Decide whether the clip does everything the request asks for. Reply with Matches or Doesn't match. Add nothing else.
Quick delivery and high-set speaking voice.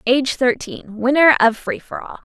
Doesn't match